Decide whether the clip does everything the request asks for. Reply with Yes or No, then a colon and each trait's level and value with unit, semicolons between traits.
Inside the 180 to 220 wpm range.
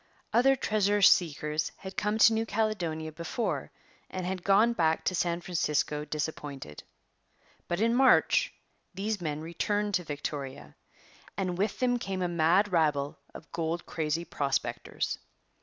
No: average, 140 wpm